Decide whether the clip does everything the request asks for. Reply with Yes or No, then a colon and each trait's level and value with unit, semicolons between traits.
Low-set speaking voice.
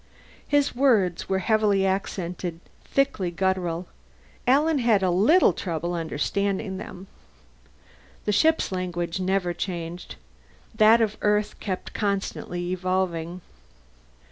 No: high, 190 Hz